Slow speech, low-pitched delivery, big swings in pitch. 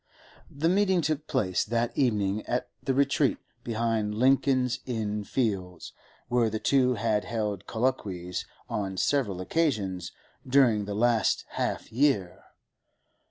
No: slow, 120 wpm; low, 115 Hz; average, 4.2 semitones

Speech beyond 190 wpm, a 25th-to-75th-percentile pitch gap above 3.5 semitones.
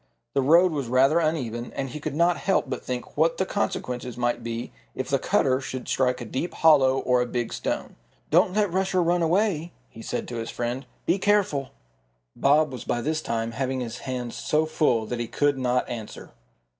Yes: average, 200 wpm; average, 4.7 semitones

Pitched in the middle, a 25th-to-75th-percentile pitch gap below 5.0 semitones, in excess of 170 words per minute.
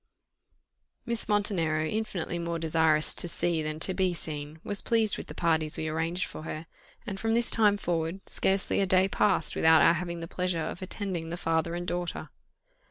Yes: medium, 170 Hz; average, 3.2 semitones; average, 185 wpm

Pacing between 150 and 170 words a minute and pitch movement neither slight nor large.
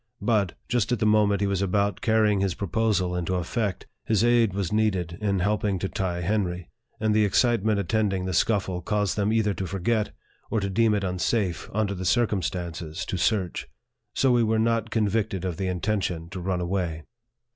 No: average, 195 wpm; average, 3.0 semitones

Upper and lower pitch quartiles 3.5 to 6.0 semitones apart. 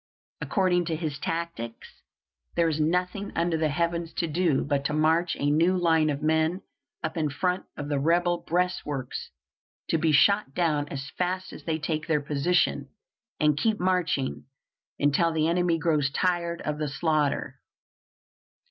No: average, 2.9 semitones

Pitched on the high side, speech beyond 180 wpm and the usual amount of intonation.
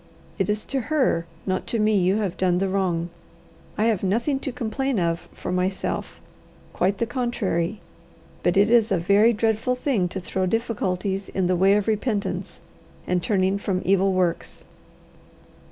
No: high, 195 Hz; average, 165 wpm; average, 3.4 semitones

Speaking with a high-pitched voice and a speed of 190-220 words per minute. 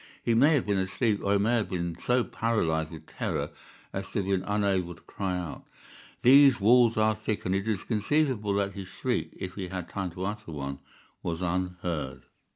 No: low, 100 Hz; average, 200 wpm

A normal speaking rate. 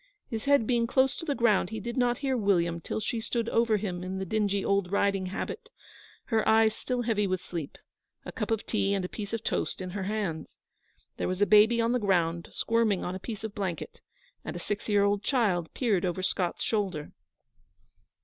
No: fast, 210 wpm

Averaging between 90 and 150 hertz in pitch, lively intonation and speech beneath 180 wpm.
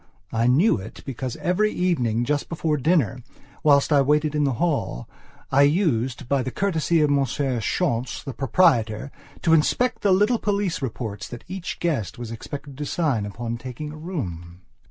Yes: medium, 140 Hz; wide, 5.7 semitones; average, 170 wpm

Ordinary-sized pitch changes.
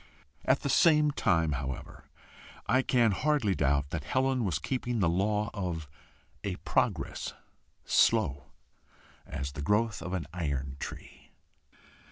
No: wide, 8.1 semitones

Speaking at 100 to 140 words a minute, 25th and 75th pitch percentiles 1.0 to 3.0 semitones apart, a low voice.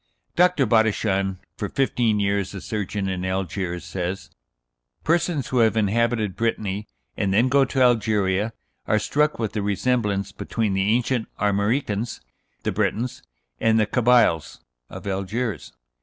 No: slow, 135 wpm; average, 3.7 semitones; low, 110 Hz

